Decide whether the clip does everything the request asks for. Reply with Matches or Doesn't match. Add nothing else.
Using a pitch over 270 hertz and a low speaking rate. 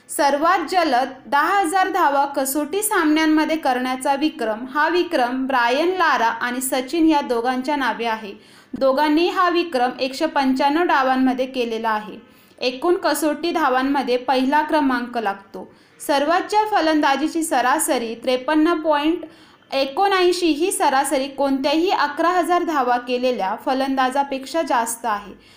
Doesn't match